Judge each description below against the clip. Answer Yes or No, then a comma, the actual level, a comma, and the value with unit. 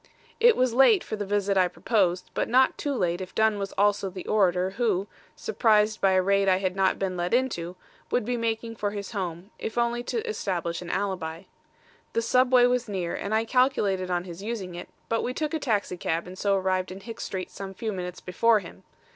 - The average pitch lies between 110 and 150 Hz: No, high, 200 Hz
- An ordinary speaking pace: No, fast, 215 wpm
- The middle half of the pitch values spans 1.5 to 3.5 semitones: No, average, 3.9 semitones